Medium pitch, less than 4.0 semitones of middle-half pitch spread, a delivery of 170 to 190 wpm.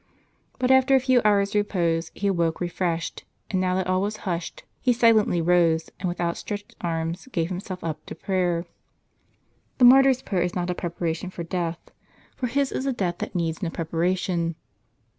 Yes: medium, 180 Hz; average, 3.6 semitones; average, 180 wpm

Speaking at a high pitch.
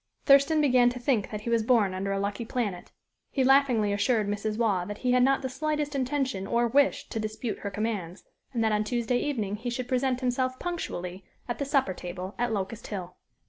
Yes: high, 235 Hz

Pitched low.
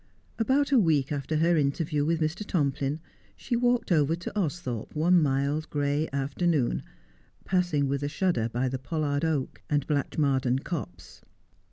No: medium, 150 Hz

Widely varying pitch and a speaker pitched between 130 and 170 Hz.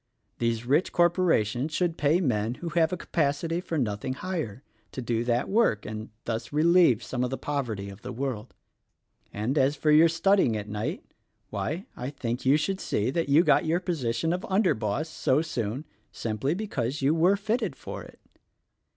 Yes: wide, 6.2 semitones; medium, 140 Hz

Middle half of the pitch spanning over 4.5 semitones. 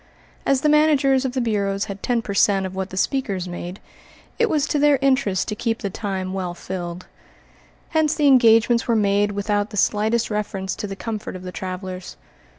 Yes: average, 5.1 semitones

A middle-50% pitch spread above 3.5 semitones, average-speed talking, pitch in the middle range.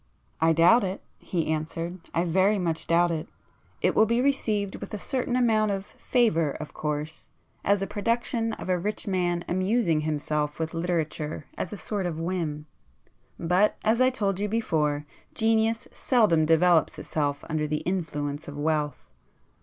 Yes: average, 5.1 semitones; average, 160 wpm; medium, 175 Hz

